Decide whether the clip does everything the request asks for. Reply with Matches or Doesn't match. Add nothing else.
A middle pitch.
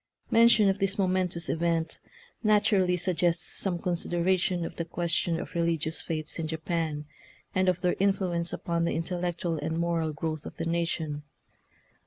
Matches